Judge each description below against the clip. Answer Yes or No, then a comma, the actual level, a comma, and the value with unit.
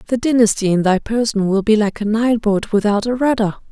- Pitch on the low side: No, high, 215 Hz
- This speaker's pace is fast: Yes, fast, 225 wpm